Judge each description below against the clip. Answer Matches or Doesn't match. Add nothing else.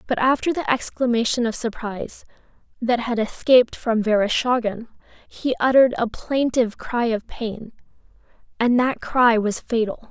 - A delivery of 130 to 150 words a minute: Matches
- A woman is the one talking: Matches